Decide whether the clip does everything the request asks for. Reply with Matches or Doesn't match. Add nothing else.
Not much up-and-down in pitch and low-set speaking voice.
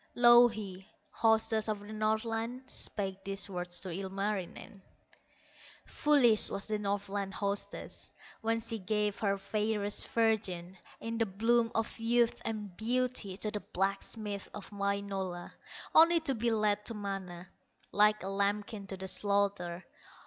Doesn't match